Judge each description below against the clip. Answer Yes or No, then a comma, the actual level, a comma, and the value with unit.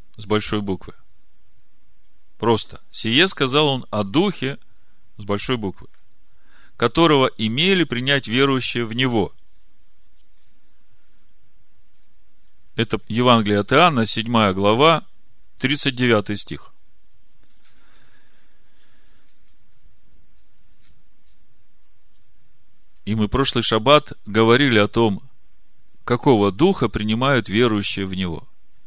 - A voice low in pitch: Yes, low, 110 Hz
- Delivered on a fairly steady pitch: No, average, 4.4 semitones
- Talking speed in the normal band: No, slow, 80 wpm